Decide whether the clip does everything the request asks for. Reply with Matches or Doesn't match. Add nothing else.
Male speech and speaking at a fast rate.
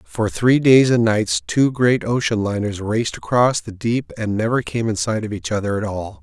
Matches